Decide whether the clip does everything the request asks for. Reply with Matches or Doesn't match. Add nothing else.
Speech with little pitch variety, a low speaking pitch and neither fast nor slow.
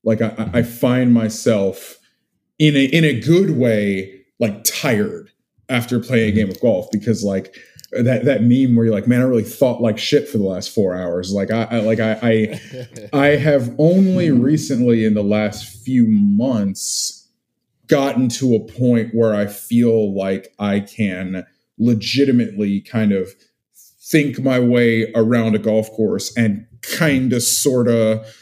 Doesn't match